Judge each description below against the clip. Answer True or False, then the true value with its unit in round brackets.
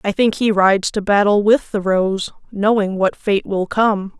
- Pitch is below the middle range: False (205 Hz)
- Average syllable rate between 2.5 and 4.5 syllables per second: True (4.4 syllables/s)